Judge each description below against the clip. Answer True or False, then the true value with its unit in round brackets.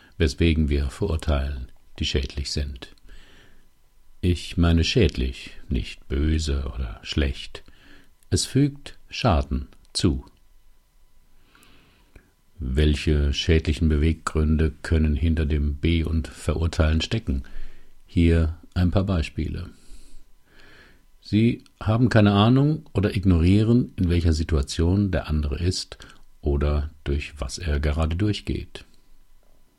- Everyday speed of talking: False (100 wpm)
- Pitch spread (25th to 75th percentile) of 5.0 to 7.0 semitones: False (3.7 semitones)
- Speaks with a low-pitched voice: True (80 Hz)